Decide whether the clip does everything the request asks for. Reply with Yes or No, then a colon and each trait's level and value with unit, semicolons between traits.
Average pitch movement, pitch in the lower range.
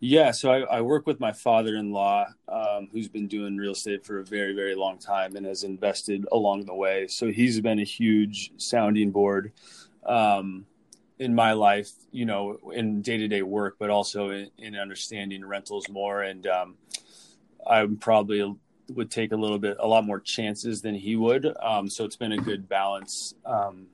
No: narrow, 1.7 semitones; low, 100 Hz